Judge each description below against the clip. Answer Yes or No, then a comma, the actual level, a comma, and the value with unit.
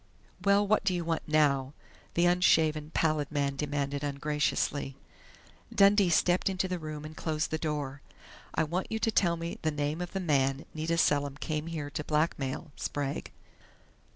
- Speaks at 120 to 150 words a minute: No, average, 165 wpm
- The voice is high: No, medium, 155 Hz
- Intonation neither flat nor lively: Yes, average, 3.1 semitones